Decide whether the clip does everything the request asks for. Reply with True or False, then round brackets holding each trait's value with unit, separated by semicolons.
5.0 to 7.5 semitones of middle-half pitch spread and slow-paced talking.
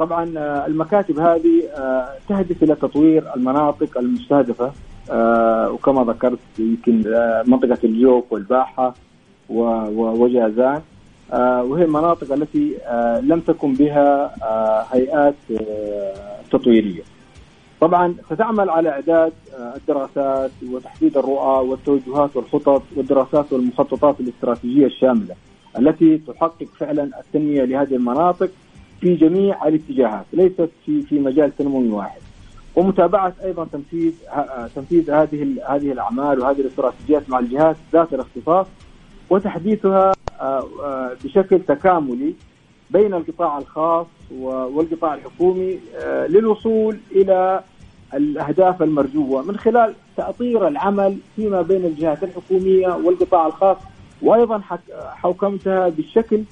True (5.5 semitones; 95 wpm)